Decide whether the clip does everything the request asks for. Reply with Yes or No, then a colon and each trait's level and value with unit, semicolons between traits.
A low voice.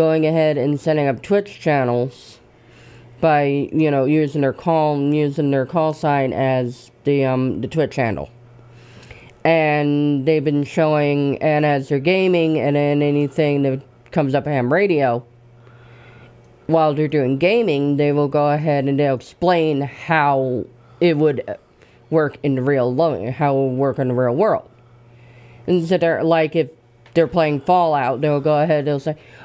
No: medium, 145 Hz